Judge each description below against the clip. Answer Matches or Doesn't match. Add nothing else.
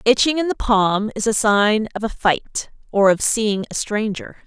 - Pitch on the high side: Matches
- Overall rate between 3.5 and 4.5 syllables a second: Matches